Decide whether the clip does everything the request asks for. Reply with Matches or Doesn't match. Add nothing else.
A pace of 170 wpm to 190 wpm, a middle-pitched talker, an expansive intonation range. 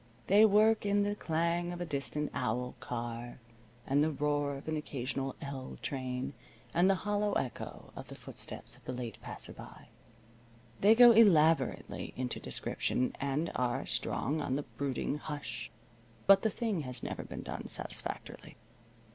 Doesn't match